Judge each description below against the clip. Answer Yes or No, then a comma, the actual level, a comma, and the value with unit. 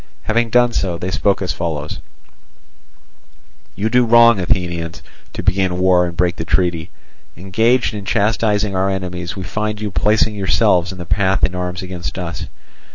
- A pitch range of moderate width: Yes, average, 3.2 semitones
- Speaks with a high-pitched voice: No, very low, 95 Hz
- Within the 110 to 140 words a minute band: No, average, 160 wpm